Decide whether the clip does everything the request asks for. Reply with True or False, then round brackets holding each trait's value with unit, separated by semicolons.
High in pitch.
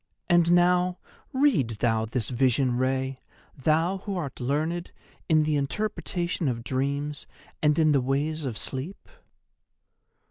False (145 Hz)